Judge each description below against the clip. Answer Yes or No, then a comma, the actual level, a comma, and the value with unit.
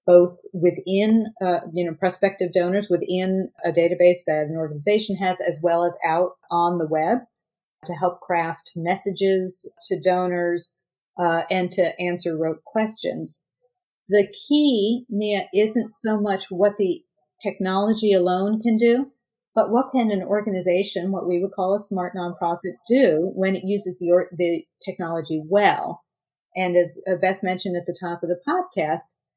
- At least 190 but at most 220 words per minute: No, average, 155 wpm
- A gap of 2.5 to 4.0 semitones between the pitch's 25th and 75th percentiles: Yes, average, 2.8 semitones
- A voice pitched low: No, medium, 185 Hz